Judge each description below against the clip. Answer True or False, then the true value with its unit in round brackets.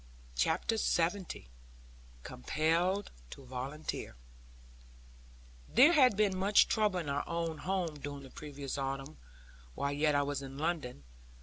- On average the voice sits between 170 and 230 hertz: False (155 Hz)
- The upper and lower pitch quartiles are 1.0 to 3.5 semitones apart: False (4.9 semitones)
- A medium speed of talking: False (125 wpm)